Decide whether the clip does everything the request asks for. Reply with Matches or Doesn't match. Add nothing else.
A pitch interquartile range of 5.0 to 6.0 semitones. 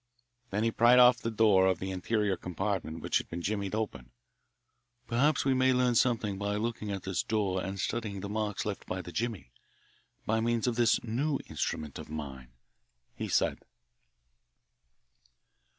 Doesn't match